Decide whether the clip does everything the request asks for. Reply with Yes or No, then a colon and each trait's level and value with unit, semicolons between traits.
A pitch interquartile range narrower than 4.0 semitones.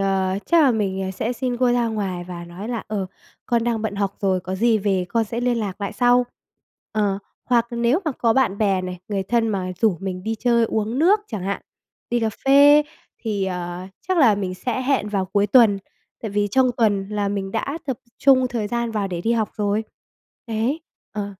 Yes: average, 3.6 semitones